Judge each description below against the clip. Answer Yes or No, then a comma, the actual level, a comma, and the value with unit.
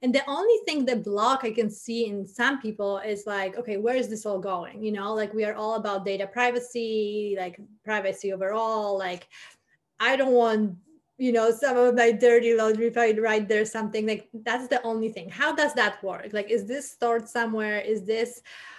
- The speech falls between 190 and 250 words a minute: Yes, average, 200 wpm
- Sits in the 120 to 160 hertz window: No, high, 220 Hz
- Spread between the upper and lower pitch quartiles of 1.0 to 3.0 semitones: Yes, narrow, 2.4 semitones